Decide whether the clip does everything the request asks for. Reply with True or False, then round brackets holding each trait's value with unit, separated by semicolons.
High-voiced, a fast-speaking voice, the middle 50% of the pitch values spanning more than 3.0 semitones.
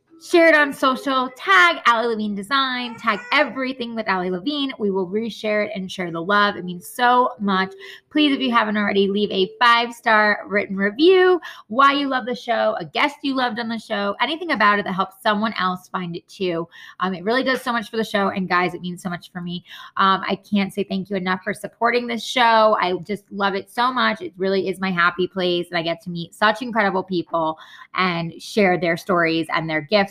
True (205 Hz; 225 wpm; 4.5 semitones)